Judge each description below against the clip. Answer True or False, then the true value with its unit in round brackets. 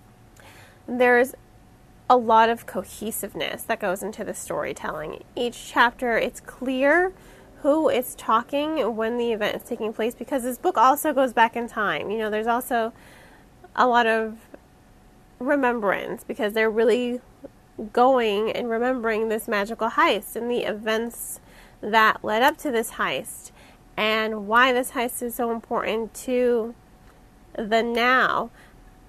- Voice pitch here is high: True (235 Hz)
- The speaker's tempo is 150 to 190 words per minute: False (140 wpm)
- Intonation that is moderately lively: False (2.1 semitones)